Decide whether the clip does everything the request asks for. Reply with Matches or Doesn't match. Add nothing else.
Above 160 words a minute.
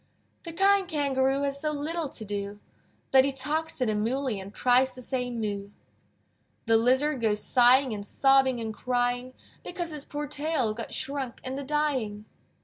Matches